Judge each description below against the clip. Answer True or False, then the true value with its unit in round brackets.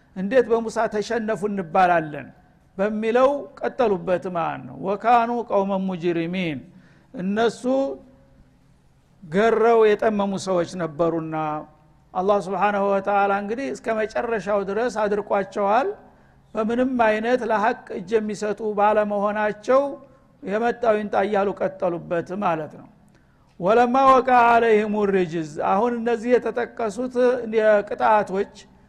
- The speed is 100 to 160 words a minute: False (85 wpm)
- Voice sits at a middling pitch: False (210 Hz)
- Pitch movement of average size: True (3.4 semitones)